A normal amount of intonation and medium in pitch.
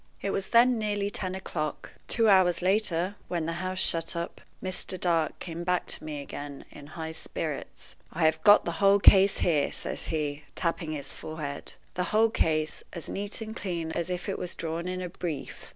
Yes: average, 3.3 semitones; medium, 175 Hz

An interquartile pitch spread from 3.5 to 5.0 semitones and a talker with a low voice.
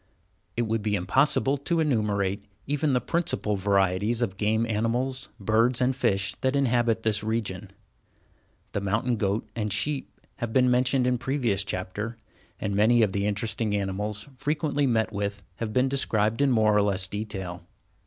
Yes: average, 3.8 semitones; low, 110 Hz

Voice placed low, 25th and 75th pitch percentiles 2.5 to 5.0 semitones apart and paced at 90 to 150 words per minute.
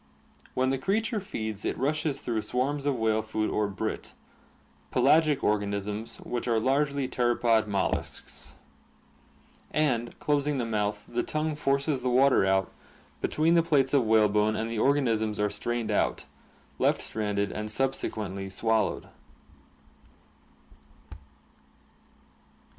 Yes: low, 120 Hz; average, 4.6 semitones; slow, 135 wpm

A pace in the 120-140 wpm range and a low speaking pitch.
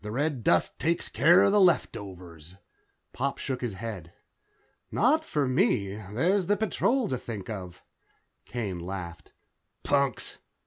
Yes: slow, 135 wpm; low, 120 Hz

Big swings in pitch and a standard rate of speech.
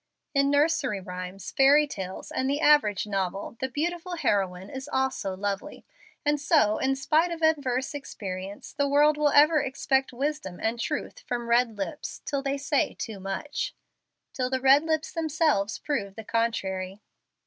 Yes: wide, 6.5 semitones; average, 160 wpm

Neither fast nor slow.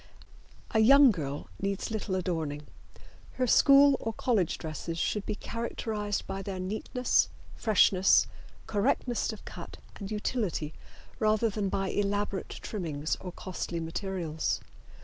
No: slow, 125 wpm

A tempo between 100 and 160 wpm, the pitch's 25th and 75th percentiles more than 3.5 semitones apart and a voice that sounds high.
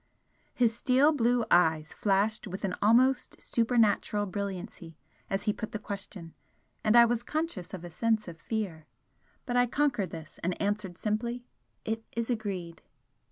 Yes: average, 155 wpm; average, 4.3 semitones; high, 215 Hz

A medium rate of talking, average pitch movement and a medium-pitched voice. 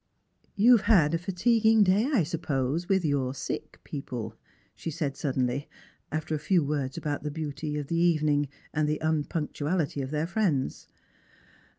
Yes: average, 175 wpm; average, 3.5 semitones; medium, 155 Hz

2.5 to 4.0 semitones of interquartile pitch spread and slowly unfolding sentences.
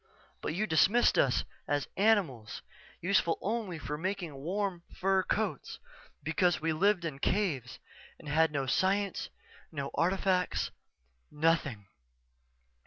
No: average, 4.7 semitones; slow, 115 wpm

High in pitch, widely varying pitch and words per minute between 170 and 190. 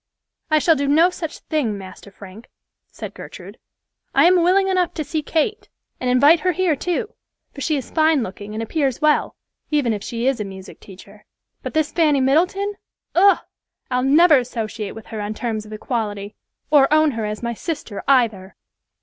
Yes: very high, 275 Hz; wide, 6.7 semitones; average, 180 wpm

